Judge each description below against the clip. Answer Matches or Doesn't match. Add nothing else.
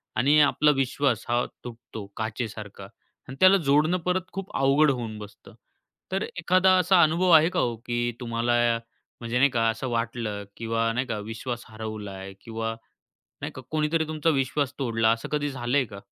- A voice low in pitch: Matches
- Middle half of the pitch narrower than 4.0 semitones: Doesn't match